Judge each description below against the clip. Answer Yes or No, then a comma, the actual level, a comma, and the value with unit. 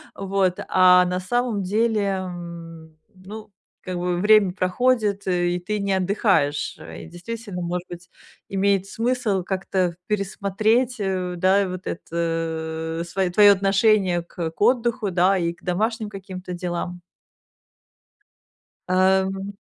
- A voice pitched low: No, high, 190 Hz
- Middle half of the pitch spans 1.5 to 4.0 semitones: Yes, narrow, 2.5 semitones